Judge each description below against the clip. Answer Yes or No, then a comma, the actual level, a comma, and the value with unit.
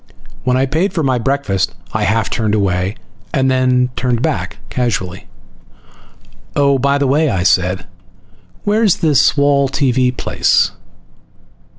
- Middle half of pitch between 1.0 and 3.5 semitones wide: No, average, 4.6 semitones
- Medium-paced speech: No, slow, 125 wpm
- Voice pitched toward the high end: No, low, 130 Hz